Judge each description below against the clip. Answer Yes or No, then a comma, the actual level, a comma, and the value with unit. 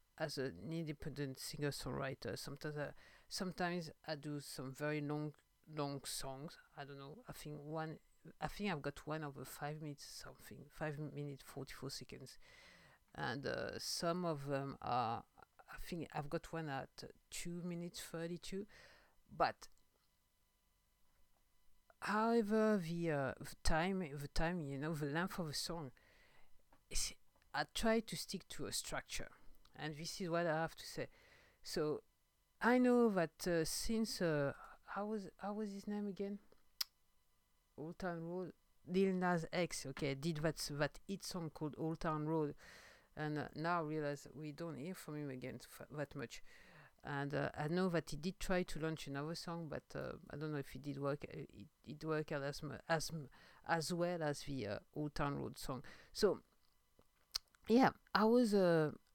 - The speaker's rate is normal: Yes, average, 165 wpm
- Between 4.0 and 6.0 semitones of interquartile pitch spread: No, average, 3.6 semitones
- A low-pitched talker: No, medium, 155 Hz